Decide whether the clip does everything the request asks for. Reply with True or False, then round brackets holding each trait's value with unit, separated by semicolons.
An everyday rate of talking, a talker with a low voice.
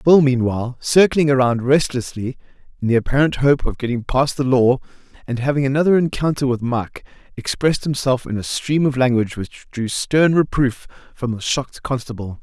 True (170 wpm; 130 Hz)